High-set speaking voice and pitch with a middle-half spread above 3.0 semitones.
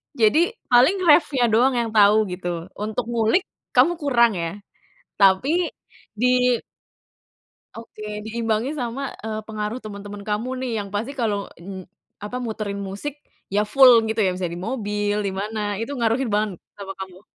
Yes: high, 220 Hz; average, 3.4 semitones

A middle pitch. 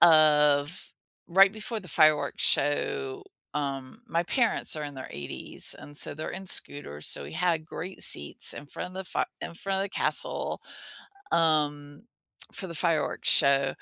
Yes: medium, 155 Hz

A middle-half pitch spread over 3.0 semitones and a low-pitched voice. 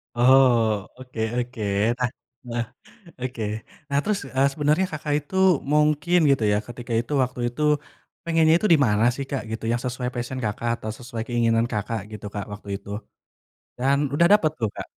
Yes: average, 4.0 semitones; low, 125 Hz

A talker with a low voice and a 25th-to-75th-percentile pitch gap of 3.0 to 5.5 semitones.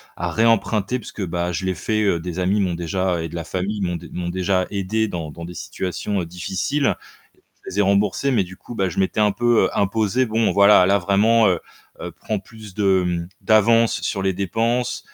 Yes: low, 100 Hz; average, 3.3 semitones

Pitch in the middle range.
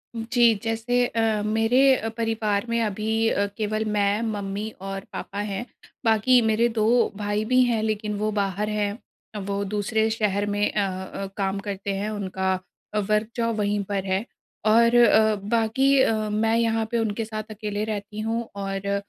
No: high, 215 Hz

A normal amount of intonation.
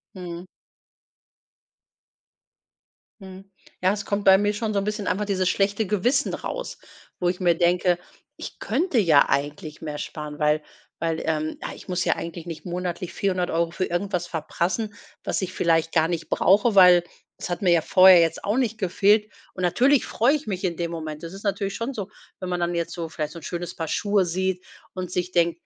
Yes: average, 3.0 semitones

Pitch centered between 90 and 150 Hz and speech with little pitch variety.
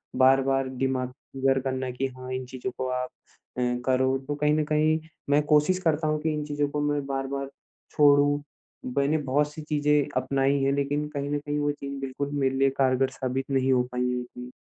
Yes: medium, 140 Hz; narrow, 2.0 semitones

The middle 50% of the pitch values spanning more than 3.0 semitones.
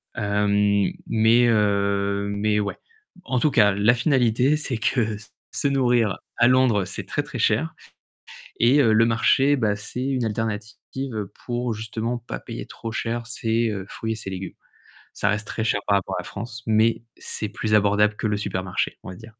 No: average, 2.7 semitones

